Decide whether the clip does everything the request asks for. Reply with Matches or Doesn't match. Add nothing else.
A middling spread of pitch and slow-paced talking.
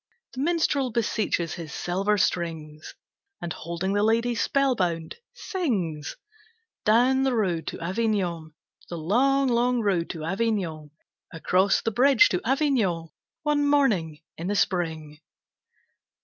Doesn't match